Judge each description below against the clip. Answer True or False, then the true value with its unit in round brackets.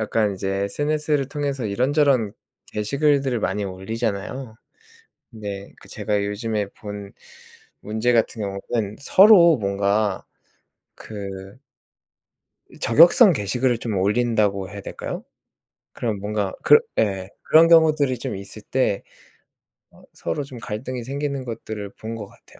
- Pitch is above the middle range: False (110 Hz)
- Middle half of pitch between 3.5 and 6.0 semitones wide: True (5.1 semitones)